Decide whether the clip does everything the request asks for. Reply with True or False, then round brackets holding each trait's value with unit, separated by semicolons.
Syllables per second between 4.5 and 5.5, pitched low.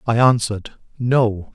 False (4.1 syllables/s; 115 Hz)